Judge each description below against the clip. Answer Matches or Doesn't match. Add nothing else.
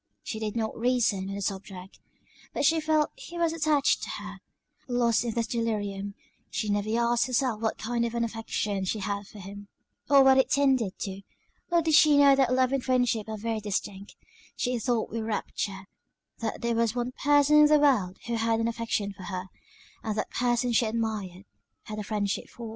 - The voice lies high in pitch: Matches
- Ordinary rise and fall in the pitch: Matches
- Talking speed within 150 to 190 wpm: Doesn't match